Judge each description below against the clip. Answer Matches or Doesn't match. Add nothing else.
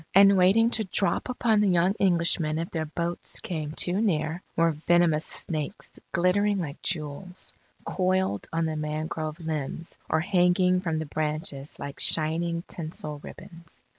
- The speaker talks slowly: Doesn't match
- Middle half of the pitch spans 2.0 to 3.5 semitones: Matches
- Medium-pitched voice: Matches